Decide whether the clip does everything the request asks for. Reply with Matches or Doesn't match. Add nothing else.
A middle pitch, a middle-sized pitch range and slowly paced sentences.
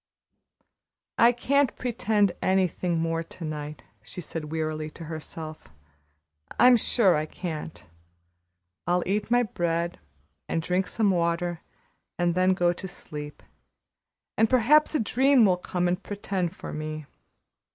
Matches